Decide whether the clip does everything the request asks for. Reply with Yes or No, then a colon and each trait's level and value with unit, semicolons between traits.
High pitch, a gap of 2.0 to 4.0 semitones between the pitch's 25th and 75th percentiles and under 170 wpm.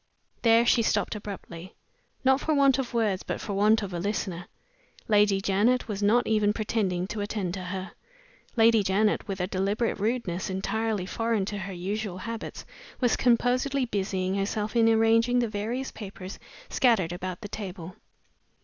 Yes: high, 210 Hz; average, 3.2 semitones; average, 160 wpm